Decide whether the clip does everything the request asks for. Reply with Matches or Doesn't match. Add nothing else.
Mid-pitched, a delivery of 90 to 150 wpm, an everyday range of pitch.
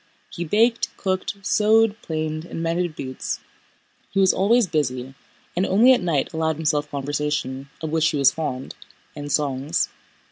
Matches